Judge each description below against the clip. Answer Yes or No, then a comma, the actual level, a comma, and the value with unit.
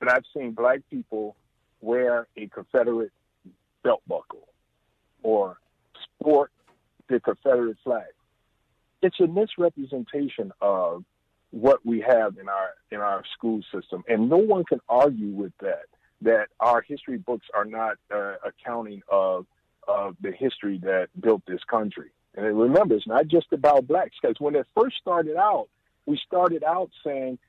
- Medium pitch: No, low, 120 Hz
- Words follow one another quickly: No, average, 150 wpm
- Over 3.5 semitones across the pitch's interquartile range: Yes, wide, 5.6 semitones